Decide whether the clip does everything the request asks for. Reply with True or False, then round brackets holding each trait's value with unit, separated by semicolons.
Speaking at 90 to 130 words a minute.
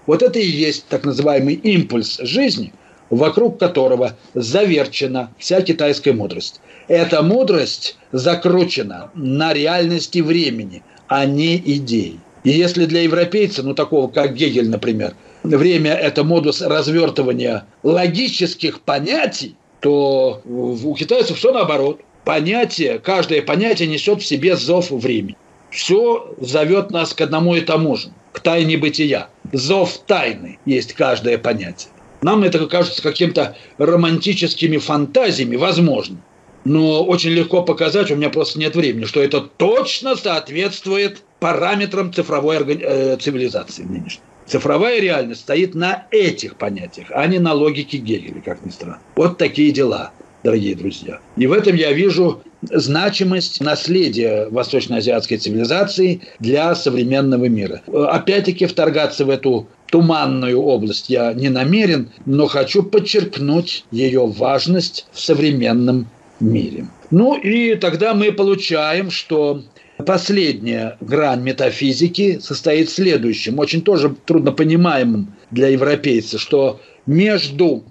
True (120 wpm)